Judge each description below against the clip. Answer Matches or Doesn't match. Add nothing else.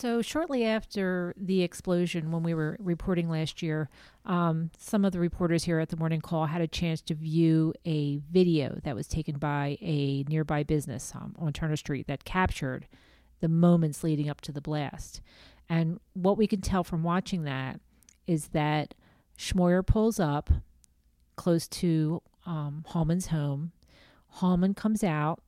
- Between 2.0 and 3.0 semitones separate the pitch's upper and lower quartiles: Matches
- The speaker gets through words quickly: Doesn't match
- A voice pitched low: Doesn't match